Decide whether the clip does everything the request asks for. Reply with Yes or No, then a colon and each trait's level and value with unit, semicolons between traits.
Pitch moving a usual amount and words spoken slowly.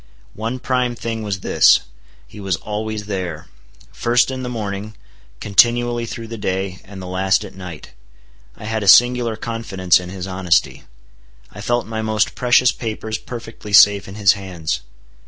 No: average, 3.5 semitones; average, 155 wpm